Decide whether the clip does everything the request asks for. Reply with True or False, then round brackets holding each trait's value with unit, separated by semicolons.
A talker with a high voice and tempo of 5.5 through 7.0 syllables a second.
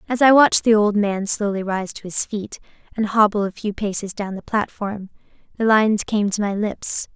False (205 Hz; 5.1 syllables/s)